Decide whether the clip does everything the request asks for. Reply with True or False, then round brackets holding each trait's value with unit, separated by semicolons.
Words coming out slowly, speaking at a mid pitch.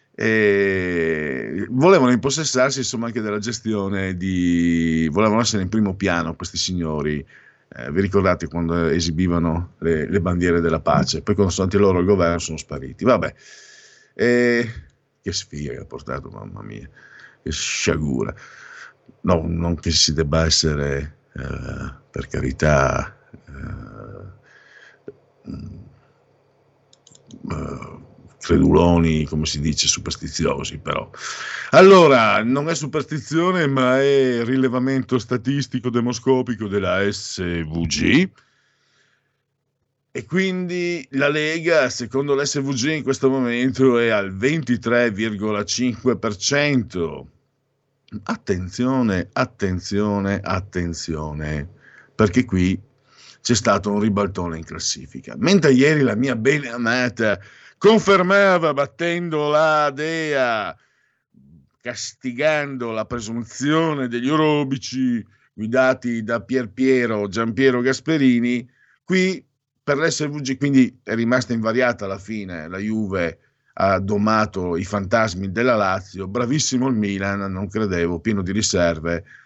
False (110 wpm; 115 Hz)